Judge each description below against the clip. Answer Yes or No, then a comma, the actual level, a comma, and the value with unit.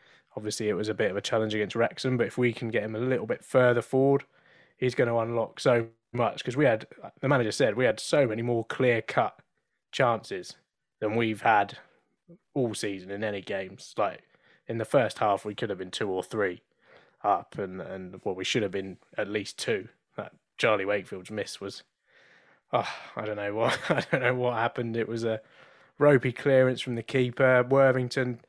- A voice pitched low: Yes, low, 120 Hz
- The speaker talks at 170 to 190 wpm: No, fast, 205 wpm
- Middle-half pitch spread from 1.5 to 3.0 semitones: Yes, average, 2.7 semitones